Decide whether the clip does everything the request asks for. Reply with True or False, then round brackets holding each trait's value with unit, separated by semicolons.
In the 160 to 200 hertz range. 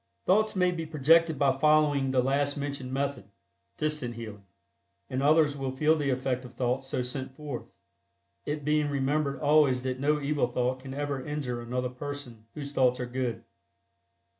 False (140 Hz)